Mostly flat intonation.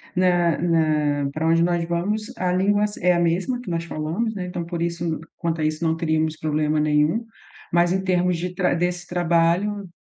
Yes: narrow, 2.1 semitones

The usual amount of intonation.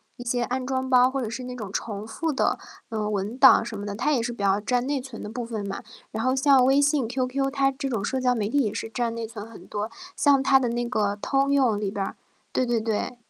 Yes: average, 3.4 semitones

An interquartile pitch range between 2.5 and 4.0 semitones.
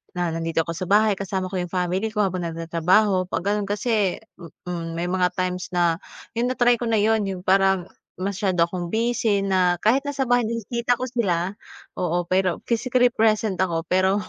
Yes: average, 3.7 semitones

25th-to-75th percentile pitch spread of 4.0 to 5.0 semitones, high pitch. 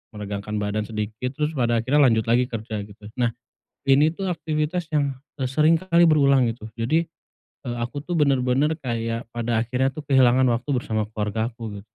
No: average, 4.6 semitones; low, 125 Hz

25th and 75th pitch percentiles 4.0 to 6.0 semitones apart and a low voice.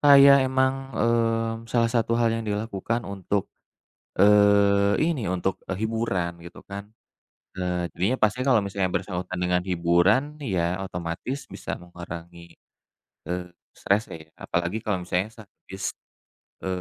Yes: average, 4.3 semitones; low, 100 Hz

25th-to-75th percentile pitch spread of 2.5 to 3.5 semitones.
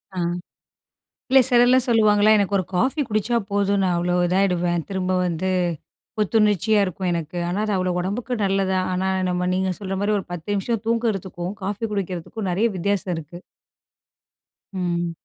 Yes: average, 2.9 semitones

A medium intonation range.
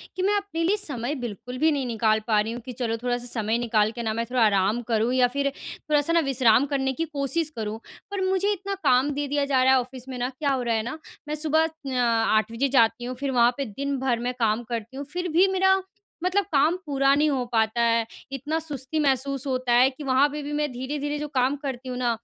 Yes: average, 3.7 semitones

